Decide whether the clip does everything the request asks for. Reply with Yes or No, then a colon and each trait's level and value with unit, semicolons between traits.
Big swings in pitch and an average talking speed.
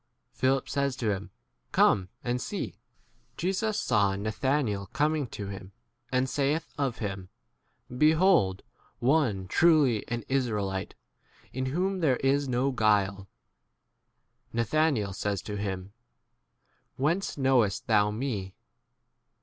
No: wide, 5.7 semitones; slow, 120 wpm